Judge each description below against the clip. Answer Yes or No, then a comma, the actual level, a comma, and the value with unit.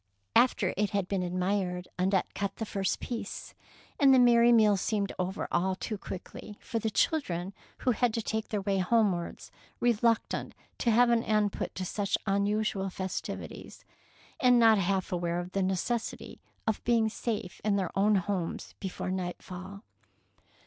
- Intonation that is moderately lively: Yes, average, 3.1 semitones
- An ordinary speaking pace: Yes, average, 165 wpm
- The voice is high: Yes, high, 200 Hz